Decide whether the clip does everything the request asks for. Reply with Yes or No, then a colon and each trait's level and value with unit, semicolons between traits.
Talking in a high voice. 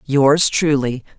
No: medium, 145 Hz